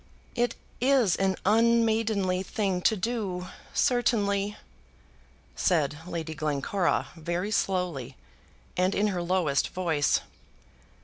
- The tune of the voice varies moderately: Yes, average, 4.0 semitones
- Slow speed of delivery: Yes, slow, 100 wpm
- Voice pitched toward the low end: No, high, 190 Hz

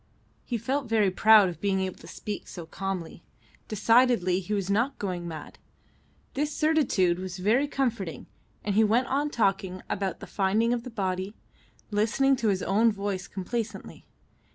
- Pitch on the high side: Yes, high, 205 Hz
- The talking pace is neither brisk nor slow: Yes, average, 160 wpm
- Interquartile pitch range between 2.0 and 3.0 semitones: No, average, 3.9 semitones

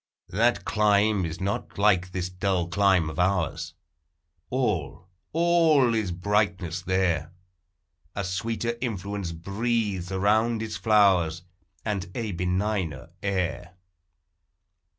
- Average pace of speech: No, slow, 105 wpm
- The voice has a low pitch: Yes, low, 100 Hz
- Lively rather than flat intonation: No, average, 3.2 semitones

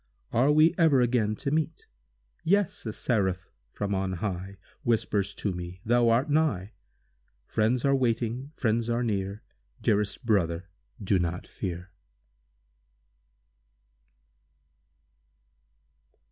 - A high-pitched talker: No, low, 110 Hz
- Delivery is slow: Yes, slow, 100 wpm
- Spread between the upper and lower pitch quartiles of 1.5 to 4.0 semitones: No, average, 4.9 semitones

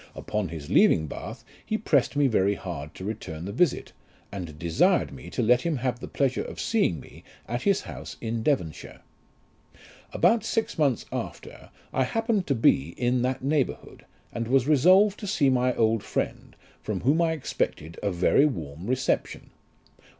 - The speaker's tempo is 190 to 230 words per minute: No, average, 170 wpm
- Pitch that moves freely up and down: Yes, wide, 7.6 semitones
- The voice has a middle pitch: No, low, 125 Hz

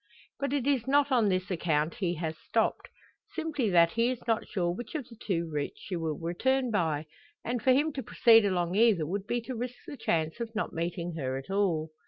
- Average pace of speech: No, fast, 220 wpm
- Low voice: No, high, 200 Hz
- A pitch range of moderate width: No, wide, 6.6 semitones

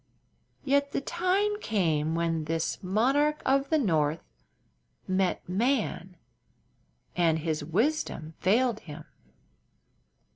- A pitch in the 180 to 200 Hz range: Yes, high, 190 Hz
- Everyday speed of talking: No, slow, 100 wpm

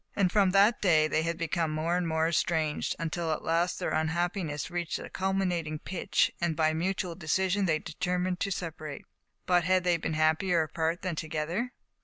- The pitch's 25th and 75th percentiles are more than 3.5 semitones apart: No, narrow, 2.5 semitones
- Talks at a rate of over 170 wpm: Yes, average, 185 wpm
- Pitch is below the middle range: No, medium, 170 Hz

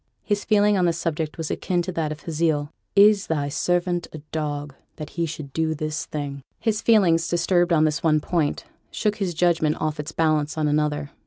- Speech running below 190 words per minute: No, average, 195 wpm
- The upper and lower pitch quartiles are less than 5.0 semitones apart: Yes, narrow, 2.6 semitones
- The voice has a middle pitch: Yes, medium, 160 Hz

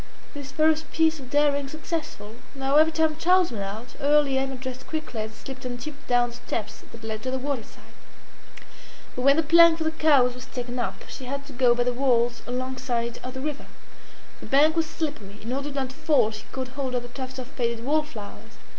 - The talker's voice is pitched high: Yes, very high, 265 Hz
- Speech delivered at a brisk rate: Yes, fast, 215 wpm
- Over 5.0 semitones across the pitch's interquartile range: No, average, 3.5 semitones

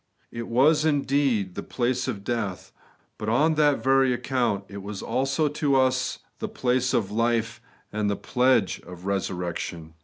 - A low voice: Yes, low, 120 Hz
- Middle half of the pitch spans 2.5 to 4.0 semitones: No, average, 4.6 semitones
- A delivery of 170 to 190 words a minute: No, average, 155 wpm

